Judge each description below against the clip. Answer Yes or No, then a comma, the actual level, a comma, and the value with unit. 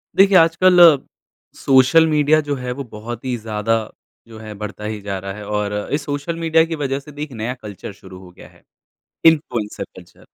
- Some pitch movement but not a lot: No, wide, 6.2 semitones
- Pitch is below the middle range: Yes, low, 125 Hz